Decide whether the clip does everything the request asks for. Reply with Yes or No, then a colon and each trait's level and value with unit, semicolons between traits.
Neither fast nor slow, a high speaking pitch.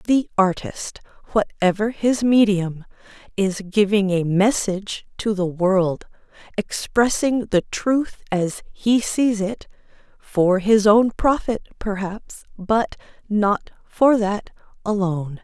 No: slow, 115 wpm; high, 205 Hz